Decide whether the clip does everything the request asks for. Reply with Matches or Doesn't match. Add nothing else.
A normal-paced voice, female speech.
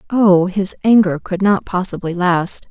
Matches